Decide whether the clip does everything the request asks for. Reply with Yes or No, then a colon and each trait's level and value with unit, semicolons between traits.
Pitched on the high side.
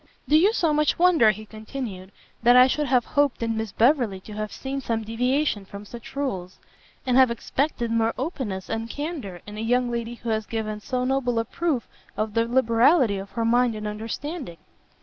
Yes: high, 235 Hz